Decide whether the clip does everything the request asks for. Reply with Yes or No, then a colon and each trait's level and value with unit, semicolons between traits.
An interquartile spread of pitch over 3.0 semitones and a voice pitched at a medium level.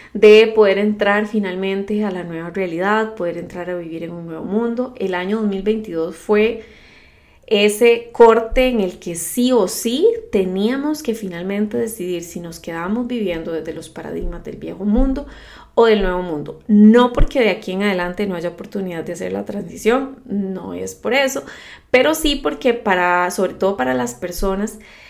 No: average, 4.4 semitones; high, 205 Hz